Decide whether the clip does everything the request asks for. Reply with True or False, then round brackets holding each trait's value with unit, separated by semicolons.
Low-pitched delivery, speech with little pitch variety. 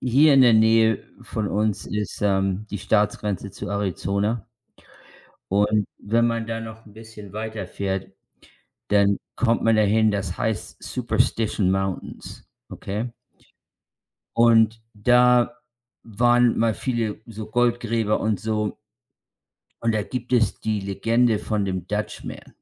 True (110 Hz; 2.1 semitones)